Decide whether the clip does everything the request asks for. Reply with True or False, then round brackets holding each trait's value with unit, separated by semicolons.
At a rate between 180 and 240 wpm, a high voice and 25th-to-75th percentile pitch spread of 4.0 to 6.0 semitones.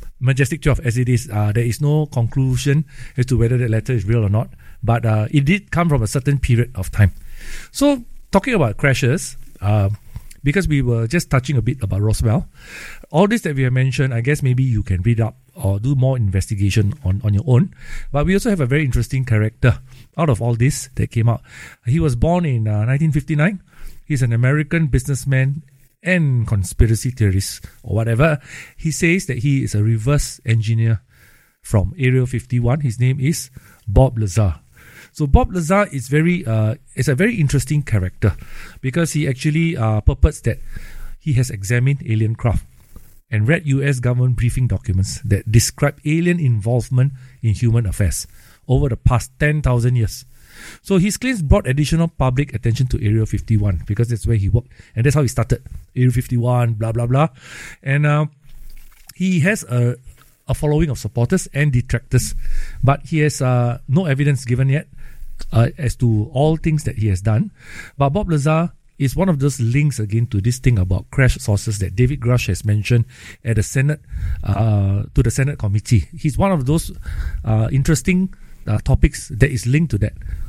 False (185 wpm; 125 Hz; 4.4 semitones)